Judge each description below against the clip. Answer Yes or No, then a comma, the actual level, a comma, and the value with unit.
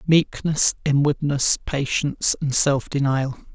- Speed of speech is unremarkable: No, slow, 100 wpm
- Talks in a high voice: No, medium, 140 Hz